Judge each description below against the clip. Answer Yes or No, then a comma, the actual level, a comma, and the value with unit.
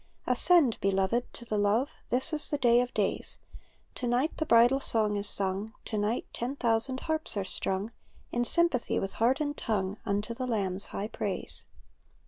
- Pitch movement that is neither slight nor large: Yes, average, 4.0 semitones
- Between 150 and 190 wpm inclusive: Yes, average, 175 wpm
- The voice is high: Yes, high, 235 Hz